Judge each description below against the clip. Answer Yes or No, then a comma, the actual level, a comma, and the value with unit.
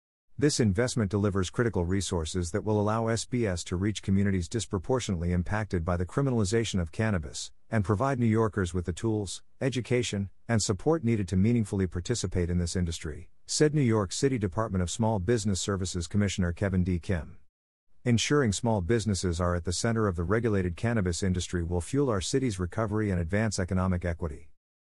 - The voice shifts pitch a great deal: No, average, 4.0 semitones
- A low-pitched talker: Yes, low, 100 Hz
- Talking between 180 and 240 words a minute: No, average, 170 wpm